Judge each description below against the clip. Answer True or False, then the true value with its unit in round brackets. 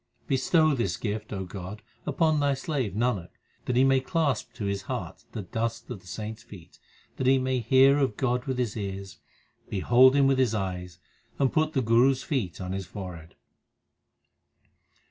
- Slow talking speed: False (180 wpm)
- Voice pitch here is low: True (120 Hz)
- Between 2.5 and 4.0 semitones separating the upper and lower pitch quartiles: False (5.3 semitones)